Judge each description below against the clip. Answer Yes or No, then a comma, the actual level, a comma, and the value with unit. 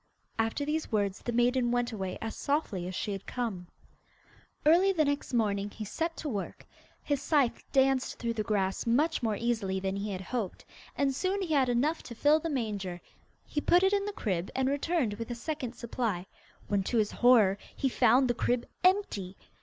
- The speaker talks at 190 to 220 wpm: Yes, average, 195 wpm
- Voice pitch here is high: Yes, high, 240 Hz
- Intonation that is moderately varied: No, wide, 5.8 semitones